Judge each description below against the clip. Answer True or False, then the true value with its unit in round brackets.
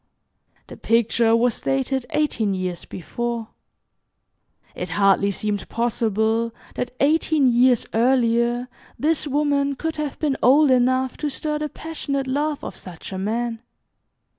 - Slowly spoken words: True (130 wpm)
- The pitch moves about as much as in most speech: True (4.0 semitones)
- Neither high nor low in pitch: False (245 Hz)